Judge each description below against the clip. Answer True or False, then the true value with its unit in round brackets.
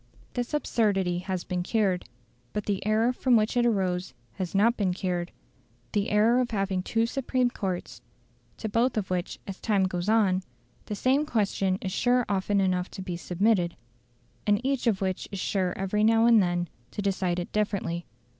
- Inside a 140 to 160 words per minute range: False (180 wpm)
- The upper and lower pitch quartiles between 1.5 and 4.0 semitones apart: True (3.5 semitones)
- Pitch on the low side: False (200 Hz)